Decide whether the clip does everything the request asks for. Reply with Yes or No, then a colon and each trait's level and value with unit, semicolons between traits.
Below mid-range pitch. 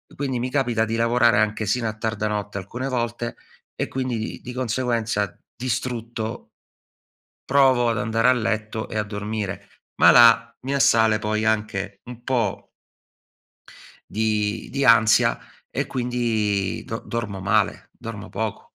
Yes: low, 115 Hz